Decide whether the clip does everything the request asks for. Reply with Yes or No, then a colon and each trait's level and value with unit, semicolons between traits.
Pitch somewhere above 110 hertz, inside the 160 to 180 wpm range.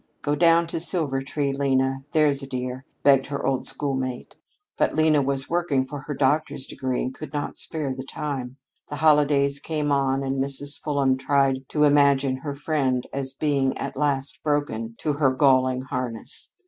Yes: medium, 140 Hz; average, 170 wpm